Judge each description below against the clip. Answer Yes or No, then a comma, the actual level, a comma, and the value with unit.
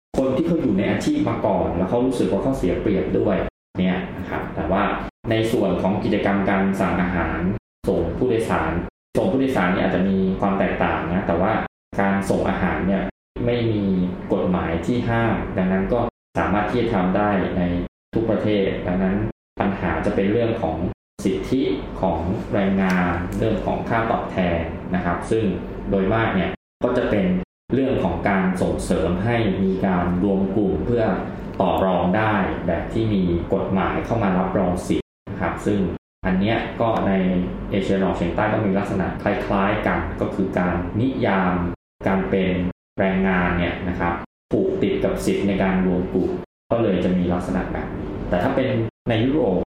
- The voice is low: Yes, very low, 95 Hz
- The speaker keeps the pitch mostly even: Yes, narrow, 2.3 semitones